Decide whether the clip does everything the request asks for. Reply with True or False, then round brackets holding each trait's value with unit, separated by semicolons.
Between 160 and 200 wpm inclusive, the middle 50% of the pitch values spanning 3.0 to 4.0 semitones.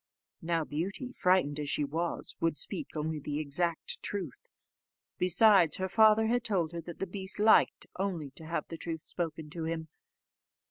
True (170 wpm; 3.5 semitones)